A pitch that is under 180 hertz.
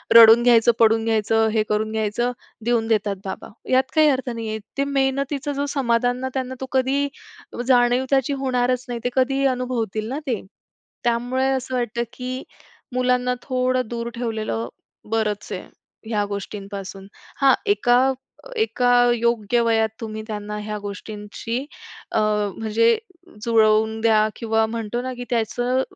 No: high, 235 Hz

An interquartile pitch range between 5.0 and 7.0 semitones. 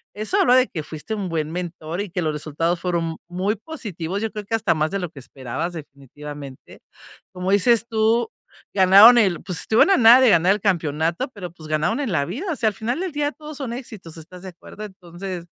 Yes: average, 5.3 semitones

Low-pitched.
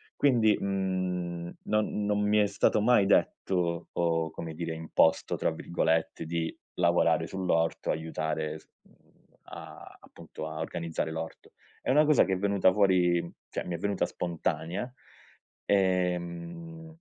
Yes: very low, 90 Hz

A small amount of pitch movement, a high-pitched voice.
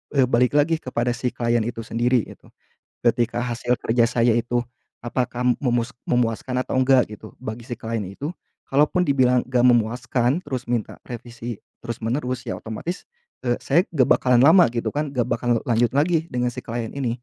No: narrow, 1.7 semitones; low, 120 Hz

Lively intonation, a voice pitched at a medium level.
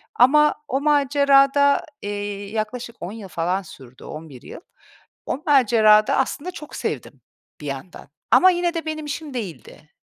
No: wide, 6.6 semitones; high, 245 Hz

